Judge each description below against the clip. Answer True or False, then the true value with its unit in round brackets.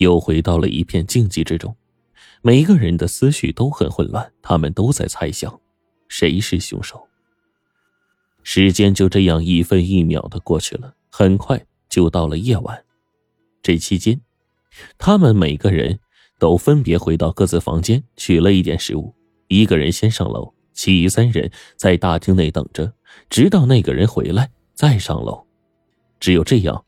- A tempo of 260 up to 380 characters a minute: False (230 characters per minute)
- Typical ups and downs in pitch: True (4.8 semitones)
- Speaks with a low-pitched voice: True (95 Hz)